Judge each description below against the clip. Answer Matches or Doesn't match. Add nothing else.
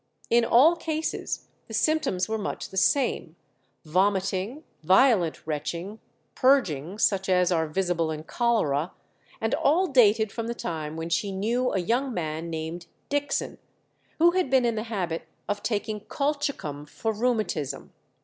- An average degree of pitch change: Doesn't match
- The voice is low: Doesn't match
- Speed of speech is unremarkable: Matches